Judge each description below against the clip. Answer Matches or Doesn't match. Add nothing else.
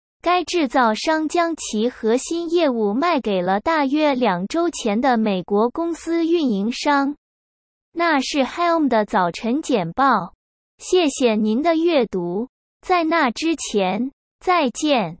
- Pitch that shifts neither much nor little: Doesn't match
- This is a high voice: Matches